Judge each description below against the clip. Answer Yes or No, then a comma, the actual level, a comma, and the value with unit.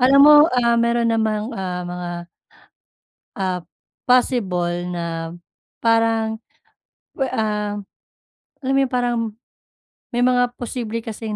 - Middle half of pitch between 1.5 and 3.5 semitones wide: No, average, 4.6 semitones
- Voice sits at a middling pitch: No, high, 225 Hz